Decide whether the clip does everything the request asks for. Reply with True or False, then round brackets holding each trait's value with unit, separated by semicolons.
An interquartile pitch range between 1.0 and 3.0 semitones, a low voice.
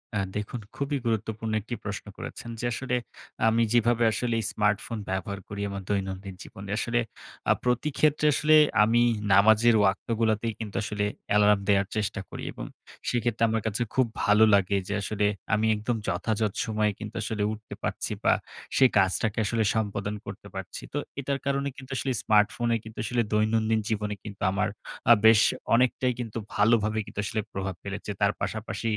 True (2.4 semitones; 110 Hz)